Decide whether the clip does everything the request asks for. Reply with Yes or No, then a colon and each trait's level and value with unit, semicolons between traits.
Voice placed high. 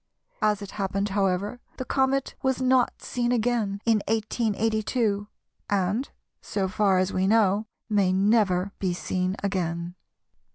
Yes: high, 205 Hz